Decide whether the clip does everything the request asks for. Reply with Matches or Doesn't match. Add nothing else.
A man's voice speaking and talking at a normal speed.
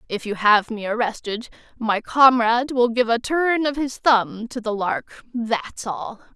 Doesn't match